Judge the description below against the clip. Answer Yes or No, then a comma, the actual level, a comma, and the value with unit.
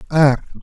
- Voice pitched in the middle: Yes, medium, 145 Hz